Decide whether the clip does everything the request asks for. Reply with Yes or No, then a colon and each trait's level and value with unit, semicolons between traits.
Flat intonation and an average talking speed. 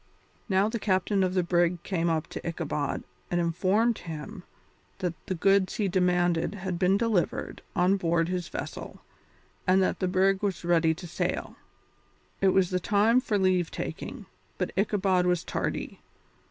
Yes: narrow, 2.1 semitones; average, 160 wpm